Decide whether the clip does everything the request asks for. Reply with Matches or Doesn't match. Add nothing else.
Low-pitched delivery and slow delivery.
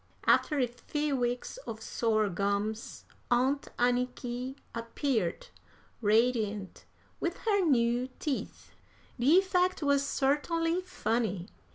Doesn't match